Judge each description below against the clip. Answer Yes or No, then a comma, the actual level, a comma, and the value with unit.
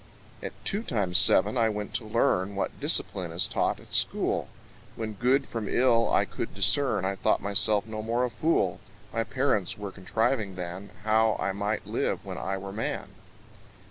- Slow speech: No, average, 175 wpm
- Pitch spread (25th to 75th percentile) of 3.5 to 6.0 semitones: No, average, 3.0 semitones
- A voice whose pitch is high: No, low, 105 Hz